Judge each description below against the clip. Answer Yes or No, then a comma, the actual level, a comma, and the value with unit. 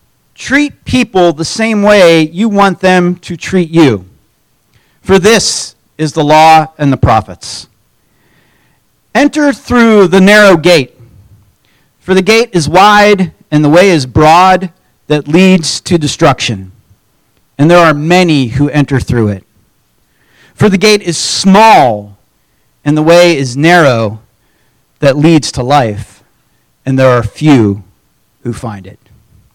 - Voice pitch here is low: No, medium, 150 Hz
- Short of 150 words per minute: Yes, slow, 135 wpm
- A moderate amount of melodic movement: No, wide, 8.5 semitones